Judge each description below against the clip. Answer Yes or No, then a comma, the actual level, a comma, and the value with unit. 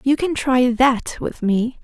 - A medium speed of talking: Yes, average, 195 wpm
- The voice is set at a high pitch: Yes, very high, 250 Hz